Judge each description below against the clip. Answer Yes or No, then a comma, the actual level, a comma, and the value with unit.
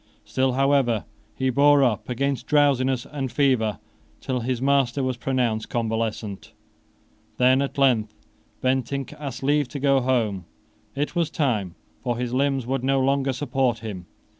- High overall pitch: No, low, 130 Hz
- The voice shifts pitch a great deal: No, narrow, 2.6 semitones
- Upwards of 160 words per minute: No, average, 145 wpm